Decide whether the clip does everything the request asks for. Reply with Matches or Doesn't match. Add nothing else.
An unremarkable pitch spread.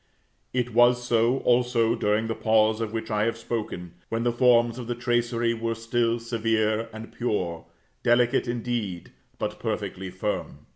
Doesn't match